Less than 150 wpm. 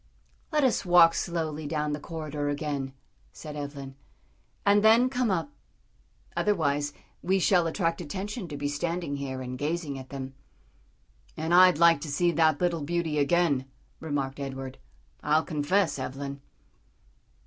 Yes: average, 140 wpm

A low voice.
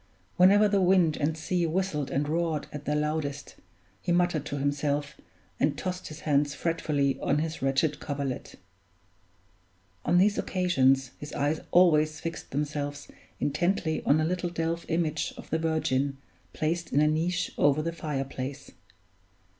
No: medium, 155 Hz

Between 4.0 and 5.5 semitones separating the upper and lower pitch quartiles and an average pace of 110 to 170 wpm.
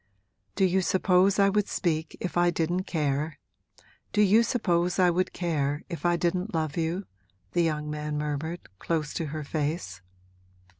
No: average, 3.2 semitones; average, 160 wpm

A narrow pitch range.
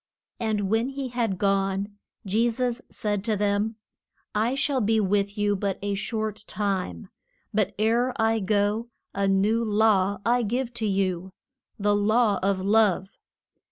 Yes: narrow, 2.2 semitones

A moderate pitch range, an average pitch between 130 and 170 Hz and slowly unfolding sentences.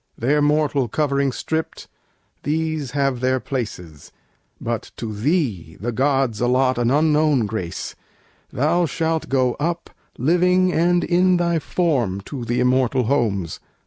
Yes: average, 4.7 semitones; low, 135 Hz; slow, 130 wpm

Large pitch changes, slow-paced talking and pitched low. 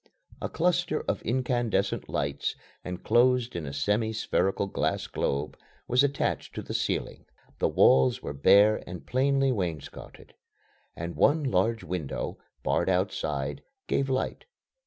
Yes: wide, 7.3 semitones; slow, 130 wpm; low, 105 Hz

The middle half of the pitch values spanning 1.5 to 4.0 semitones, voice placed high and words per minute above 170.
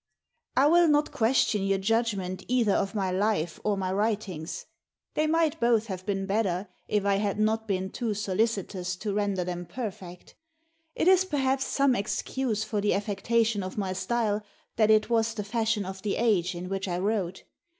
Yes: average, 3.1 semitones; high, 210 Hz; average, 190 wpm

